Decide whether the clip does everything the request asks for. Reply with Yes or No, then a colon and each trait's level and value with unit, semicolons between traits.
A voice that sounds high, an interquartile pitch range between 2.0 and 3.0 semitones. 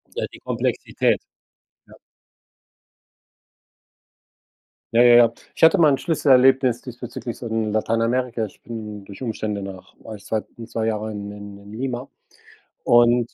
No: low, 115 Hz; average, 2.7 semitones